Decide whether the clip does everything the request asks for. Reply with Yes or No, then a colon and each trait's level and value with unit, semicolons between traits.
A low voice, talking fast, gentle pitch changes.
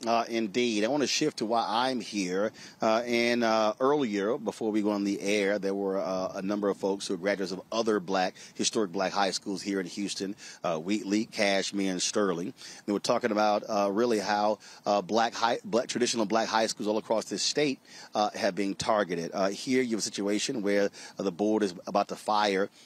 Yes: low, 105 Hz; fast, 215 wpm; narrow, 2.1 semitones